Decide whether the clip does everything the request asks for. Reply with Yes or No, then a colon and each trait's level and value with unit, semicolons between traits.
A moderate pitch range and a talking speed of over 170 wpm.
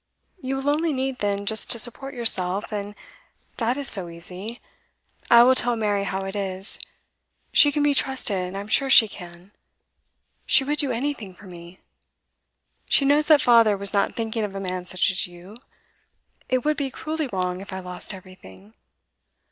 No: wide, 5.8 semitones; average, 180 wpm